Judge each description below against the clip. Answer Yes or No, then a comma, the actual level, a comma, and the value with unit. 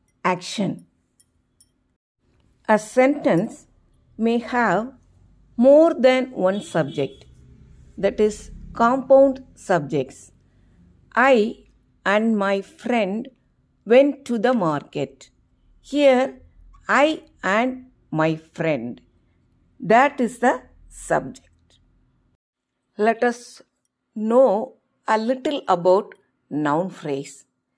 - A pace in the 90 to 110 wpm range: No, average, 80 wpm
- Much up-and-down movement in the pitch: Yes, wide, 8.0 semitones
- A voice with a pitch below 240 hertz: Yes, high, 215 Hz